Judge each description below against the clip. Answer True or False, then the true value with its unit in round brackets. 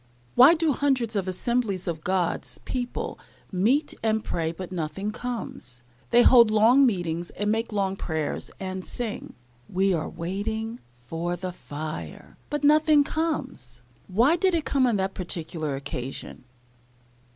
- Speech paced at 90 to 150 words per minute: True (140 wpm)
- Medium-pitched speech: False (195 Hz)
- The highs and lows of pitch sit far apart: True (6.3 semitones)